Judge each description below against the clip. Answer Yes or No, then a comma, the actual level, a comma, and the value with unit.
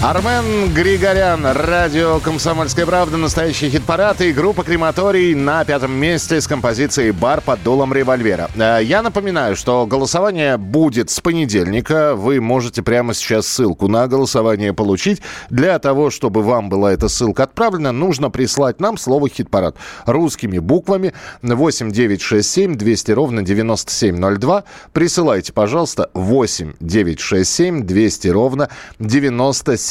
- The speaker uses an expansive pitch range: Yes, wide, 6.7 semitones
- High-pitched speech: No, low, 135 Hz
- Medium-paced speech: Yes, average, 130 wpm